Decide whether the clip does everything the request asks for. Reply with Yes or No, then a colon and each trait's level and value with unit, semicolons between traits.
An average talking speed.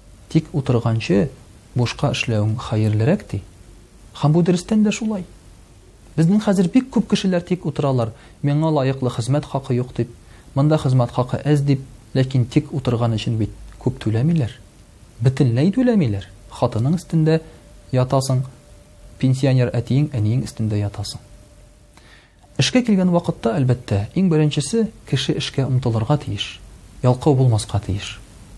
Yes: average, 120 wpm